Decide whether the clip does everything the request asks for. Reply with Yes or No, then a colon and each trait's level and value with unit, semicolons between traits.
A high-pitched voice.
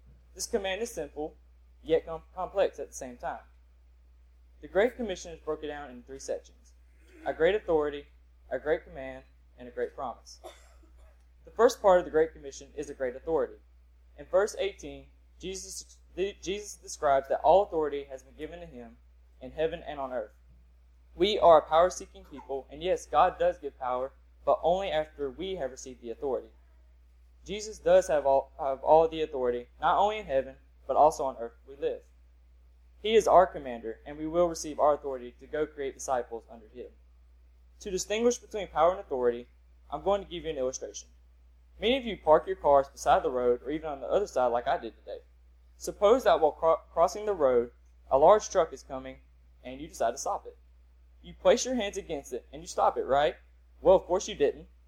No: low, 135 Hz